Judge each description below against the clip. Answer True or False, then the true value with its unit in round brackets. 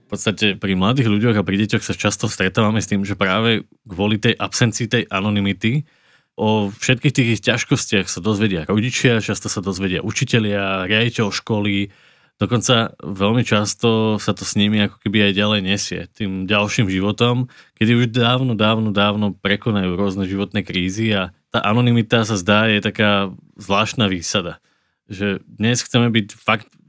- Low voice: True (105 Hz)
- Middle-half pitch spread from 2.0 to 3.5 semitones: True (2.5 semitones)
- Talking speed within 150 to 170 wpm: True (160 wpm)